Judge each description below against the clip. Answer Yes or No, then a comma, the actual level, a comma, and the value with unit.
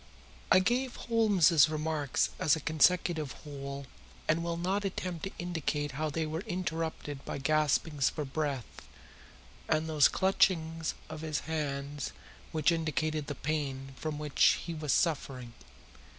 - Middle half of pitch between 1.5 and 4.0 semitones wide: Yes, narrow, 2.5 semitones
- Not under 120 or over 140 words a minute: Yes, slow, 135 wpm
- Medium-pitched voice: Yes, medium, 155 Hz